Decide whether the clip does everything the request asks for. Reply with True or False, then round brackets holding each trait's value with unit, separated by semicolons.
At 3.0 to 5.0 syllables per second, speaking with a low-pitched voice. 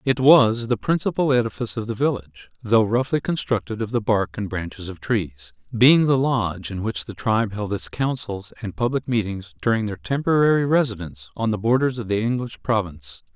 False (5.5 syllables/s; 110 Hz)